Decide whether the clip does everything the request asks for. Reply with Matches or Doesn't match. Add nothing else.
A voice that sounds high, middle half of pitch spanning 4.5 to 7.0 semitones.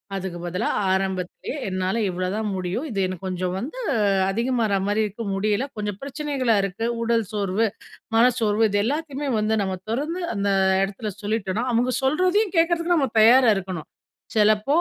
Matches